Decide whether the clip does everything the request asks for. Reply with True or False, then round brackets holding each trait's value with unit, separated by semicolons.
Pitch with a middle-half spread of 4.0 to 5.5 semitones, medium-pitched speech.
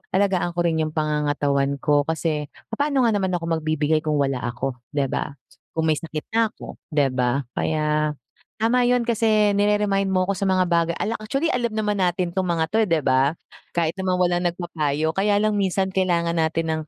True (4.9 semitones; 170 Hz)